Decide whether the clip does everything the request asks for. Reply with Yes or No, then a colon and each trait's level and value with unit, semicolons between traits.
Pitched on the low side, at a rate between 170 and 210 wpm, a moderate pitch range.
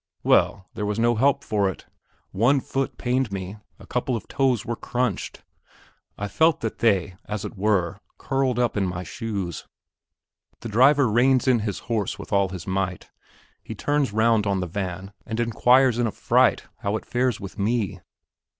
Yes: low, 110 Hz; average, 175 wpm; average, 4.0 semitones